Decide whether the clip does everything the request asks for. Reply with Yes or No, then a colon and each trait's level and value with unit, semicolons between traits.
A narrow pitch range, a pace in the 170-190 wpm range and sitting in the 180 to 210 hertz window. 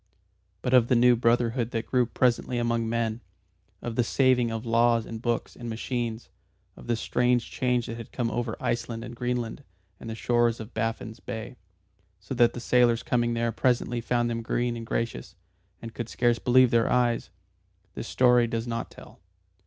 No: narrow, 1.1 semitones; average, 180 wpm; low, 120 Hz